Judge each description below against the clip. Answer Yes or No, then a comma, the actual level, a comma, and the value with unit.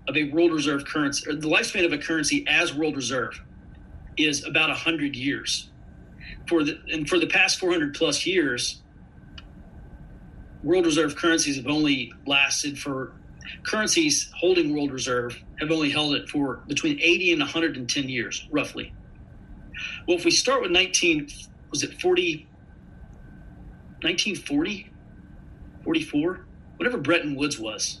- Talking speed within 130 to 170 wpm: Yes, average, 140 wpm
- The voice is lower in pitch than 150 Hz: No, medium, 155 Hz